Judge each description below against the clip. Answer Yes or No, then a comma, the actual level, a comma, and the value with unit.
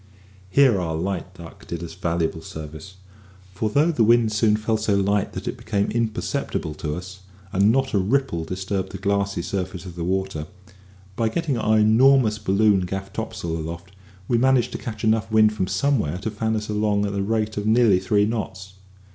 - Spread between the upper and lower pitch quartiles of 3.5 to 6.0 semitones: No, average, 3.1 semitones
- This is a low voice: Yes, low, 100 Hz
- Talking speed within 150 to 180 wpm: No, average, 190 wpm